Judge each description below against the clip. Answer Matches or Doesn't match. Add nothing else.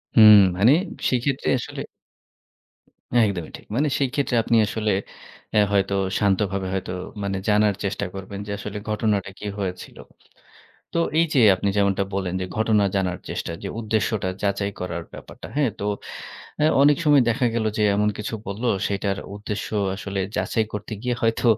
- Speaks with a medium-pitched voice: Doesn't match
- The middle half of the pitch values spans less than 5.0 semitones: Matches